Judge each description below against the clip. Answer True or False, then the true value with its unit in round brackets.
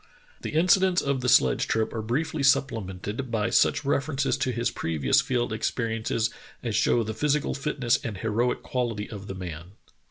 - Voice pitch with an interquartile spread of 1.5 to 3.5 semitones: False (4.4 semitones)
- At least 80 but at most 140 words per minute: False (165 wpm)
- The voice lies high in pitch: False (115 Hz)